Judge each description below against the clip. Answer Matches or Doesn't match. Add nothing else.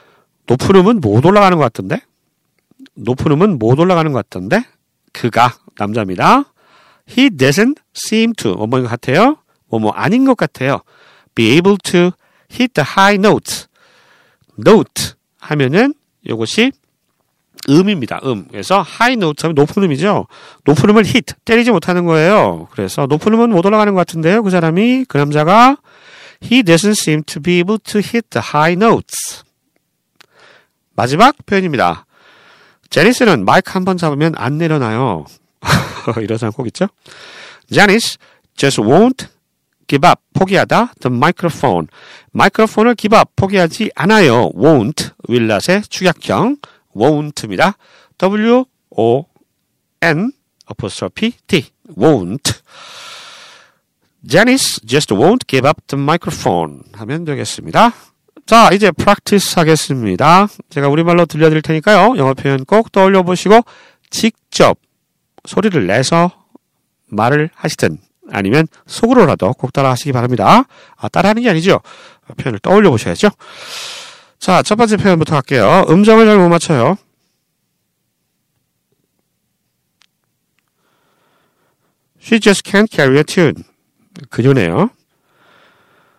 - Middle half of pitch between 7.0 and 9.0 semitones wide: Matches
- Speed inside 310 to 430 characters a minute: Matches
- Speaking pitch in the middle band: Matches